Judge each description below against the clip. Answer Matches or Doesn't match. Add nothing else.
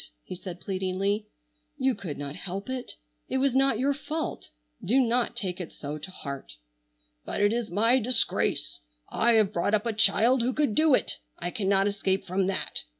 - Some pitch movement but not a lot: Matches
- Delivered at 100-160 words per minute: Doesn't match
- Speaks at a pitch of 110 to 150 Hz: Doesn't match